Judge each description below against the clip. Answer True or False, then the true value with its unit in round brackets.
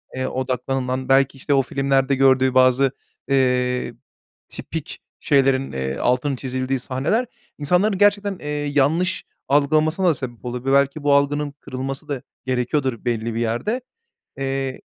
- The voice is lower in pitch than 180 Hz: True (135 Hz)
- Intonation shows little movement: True (2.1 semitones)